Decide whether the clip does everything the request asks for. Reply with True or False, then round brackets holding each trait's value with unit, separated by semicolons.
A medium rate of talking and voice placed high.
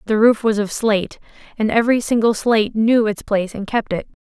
False (210 wpm; 220 Hz)